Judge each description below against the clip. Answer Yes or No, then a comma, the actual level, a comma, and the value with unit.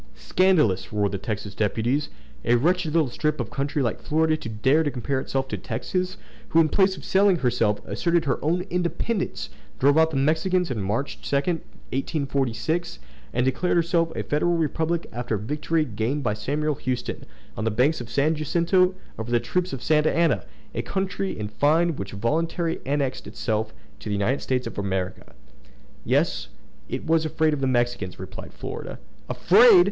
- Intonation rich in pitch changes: Yes, wide, 5.9 semitones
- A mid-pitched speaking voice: Yes, medium, 145 Hz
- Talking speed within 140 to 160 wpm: No, average, 175 wpm